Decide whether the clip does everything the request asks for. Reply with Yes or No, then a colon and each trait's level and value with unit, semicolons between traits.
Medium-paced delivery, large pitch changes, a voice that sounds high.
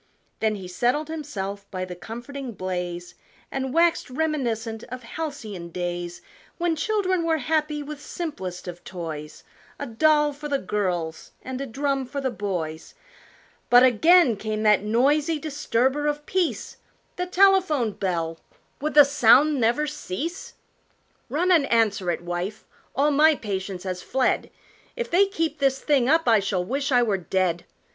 Yes: average, 150 wpm; wide, 7.7 semitones; very high, 250 Hz